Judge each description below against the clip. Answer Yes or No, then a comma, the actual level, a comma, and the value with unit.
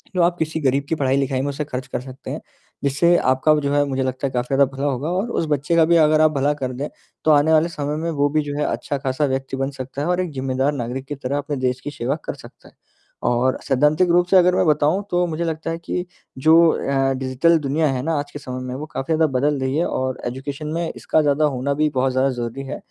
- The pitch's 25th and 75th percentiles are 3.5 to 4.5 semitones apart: No, average, 2.9 semitones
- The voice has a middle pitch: Yes, medium, 145 Hz